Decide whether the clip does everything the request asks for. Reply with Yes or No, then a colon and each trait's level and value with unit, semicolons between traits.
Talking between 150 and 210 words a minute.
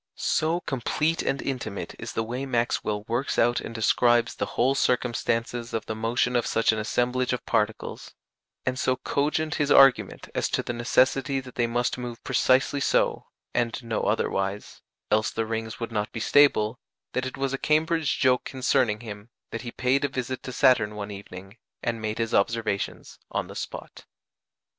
Yes: average, 175 wpm